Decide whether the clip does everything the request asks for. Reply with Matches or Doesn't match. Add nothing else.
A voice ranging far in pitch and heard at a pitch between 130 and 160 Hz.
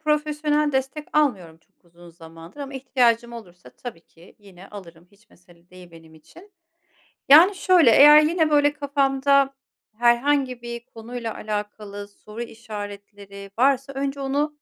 Doesn't match